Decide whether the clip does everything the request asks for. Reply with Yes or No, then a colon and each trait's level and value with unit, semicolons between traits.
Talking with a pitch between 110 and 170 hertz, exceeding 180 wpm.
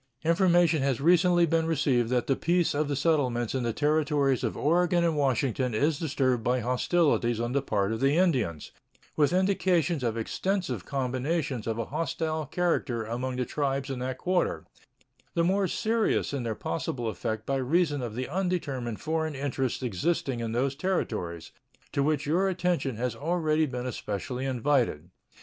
No: medium, 140 Hz; average, 165 wpm